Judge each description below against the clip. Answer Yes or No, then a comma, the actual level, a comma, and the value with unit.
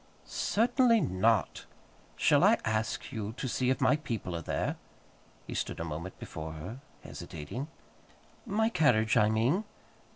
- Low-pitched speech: Yes, low, 110 Hz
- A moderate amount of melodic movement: No, wide, 8.2 semitones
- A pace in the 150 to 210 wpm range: No, average, 140 wpm